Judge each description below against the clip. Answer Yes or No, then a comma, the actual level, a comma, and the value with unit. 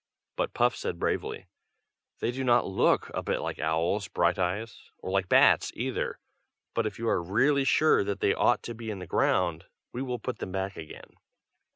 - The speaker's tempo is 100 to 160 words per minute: No, average, 190 wpm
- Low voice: Yes, low, 100 Hz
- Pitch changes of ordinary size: Yes, average, 4.9 semitones